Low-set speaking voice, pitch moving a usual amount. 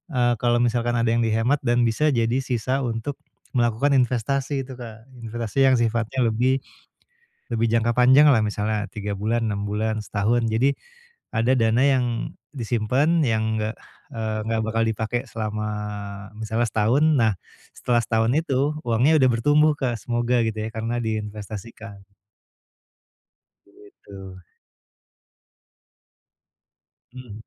No: low, 115 Hz; narrow, 2.3 semitones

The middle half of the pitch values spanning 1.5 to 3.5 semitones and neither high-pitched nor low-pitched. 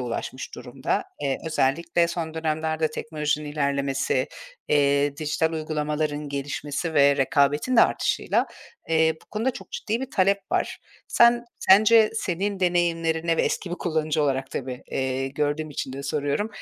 Yes: average, 3.1 semitones; medium, 155 Hz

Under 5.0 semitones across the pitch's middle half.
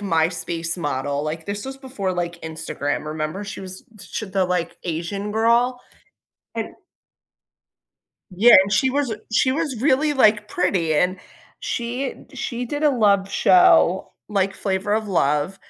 No: wide, 5.5 semitones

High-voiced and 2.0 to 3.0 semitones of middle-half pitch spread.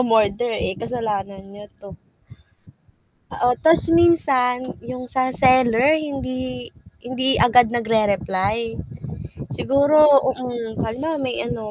Yes: high, 245 Hz; narrow, 2.6 semitones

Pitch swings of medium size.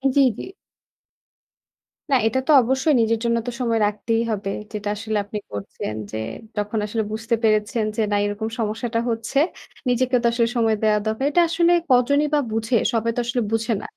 No: narrow, 2.3 semitones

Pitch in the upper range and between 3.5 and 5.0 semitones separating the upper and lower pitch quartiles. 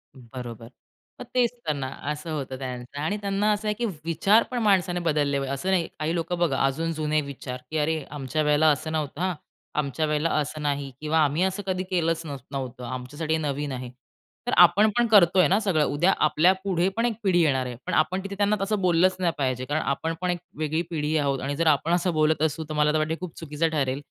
No: medium, 155 Hz; average, 4.0 semitones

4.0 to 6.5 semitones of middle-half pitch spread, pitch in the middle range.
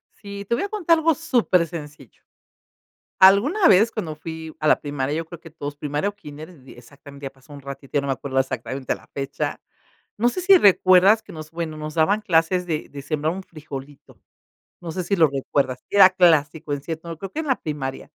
Yes: average, 5.1 semitones; medium, 160 Hz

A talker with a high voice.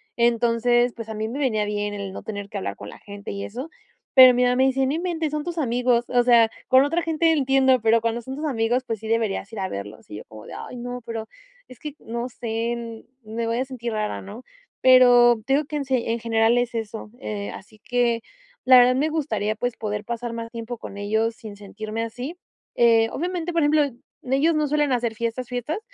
Yes: high, 235 Hz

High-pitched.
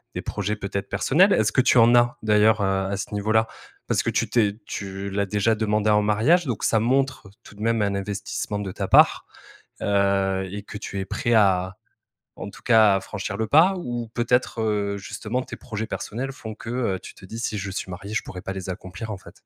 No: low, 105 Hz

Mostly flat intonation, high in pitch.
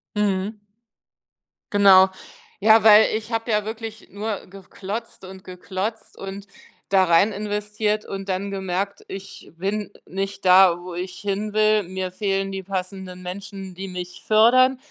Yes: narrow, 2.0 semitones; high, 195 Hz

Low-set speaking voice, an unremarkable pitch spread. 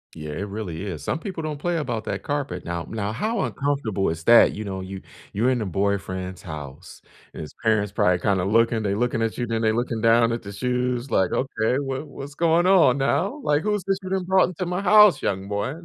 No: low, 115 Hz; wide, 6.8 semitones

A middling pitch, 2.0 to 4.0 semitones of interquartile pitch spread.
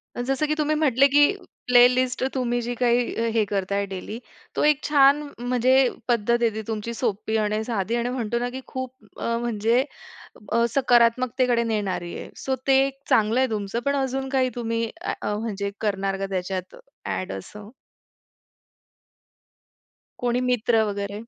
No: high, 235 Hz; average, 3.4 semitones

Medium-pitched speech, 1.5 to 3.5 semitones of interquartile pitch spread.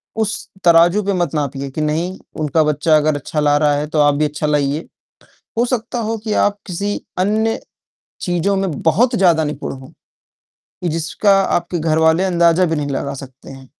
No: medium, 165 Hz; average, 4.4 semitones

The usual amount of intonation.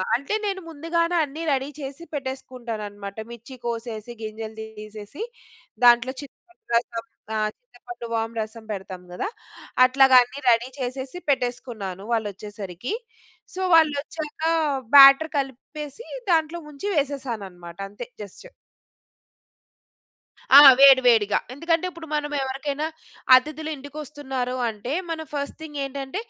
Yes: average, 4.8 semitones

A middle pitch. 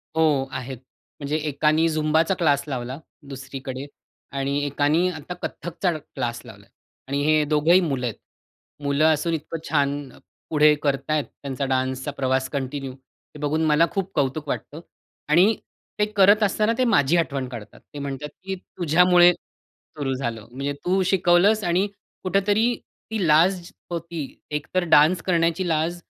Yes: medium, 155 Hz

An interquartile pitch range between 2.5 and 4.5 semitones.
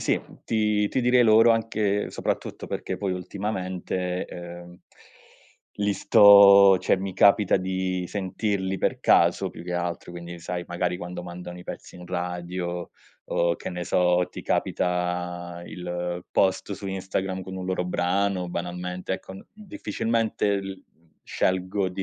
No: narrow, 2.1 semitones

